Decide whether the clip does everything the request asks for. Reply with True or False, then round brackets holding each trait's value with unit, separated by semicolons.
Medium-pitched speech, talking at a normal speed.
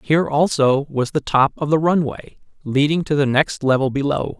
True (145 Hz; 190 wpm)